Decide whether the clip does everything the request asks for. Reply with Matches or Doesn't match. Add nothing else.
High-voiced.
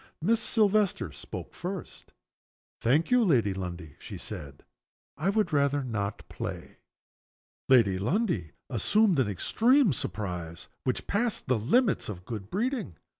Doesn't match